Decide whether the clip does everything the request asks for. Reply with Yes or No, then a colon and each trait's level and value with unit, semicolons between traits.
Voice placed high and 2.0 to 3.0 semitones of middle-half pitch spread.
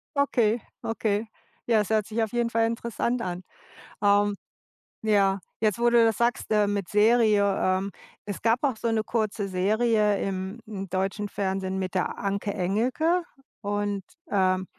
Yes: high, 210 Hz; average, 2.7 semitones